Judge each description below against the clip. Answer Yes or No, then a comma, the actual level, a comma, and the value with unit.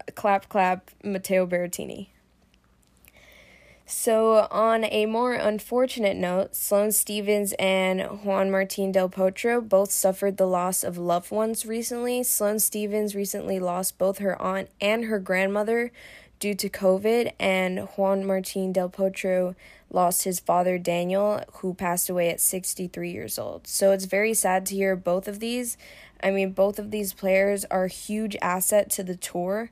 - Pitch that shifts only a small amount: Yes, narrow, 2.1 semitones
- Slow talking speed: No, average, 155 wpm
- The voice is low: No, high, 195 Hz